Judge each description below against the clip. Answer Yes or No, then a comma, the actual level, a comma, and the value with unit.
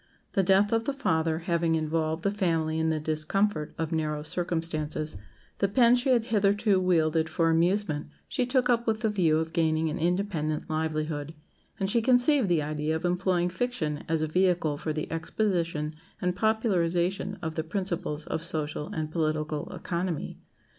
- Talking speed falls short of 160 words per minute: No, average, 165 wpm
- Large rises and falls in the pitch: No, average, 4.0 semitones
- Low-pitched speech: No, medium, 165 Hz